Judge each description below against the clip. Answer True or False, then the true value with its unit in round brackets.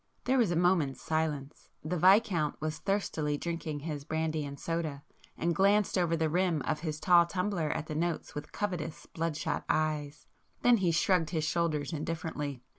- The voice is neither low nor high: True (160 Hz)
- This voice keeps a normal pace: True (165 wpm)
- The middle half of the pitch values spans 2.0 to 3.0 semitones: True (2.7 semitones)